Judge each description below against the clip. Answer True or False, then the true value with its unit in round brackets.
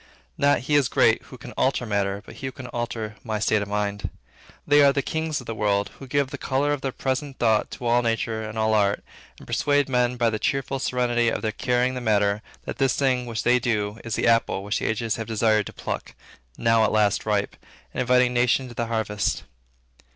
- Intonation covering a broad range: False (3.1 semitones)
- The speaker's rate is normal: False (225 wpm)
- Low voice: True (115 Hz)